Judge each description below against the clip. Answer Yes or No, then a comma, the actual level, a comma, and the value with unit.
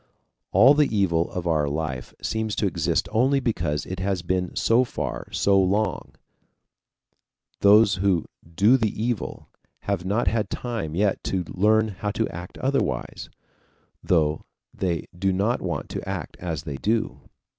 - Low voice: Yes, low, 100 Hz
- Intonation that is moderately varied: Yes, average, 4.1 semitones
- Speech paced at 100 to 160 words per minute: Yes, average, 150 wpm